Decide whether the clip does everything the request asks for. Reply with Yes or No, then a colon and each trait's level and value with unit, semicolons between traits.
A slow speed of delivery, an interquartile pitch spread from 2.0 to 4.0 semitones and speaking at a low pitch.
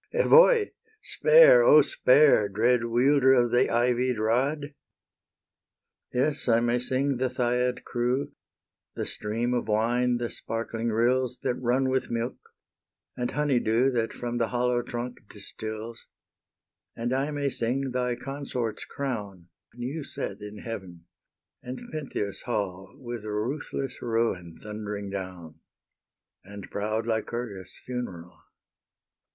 Yes: slow, 125 wpm; average, 3.0 semitones; low, 120 Hz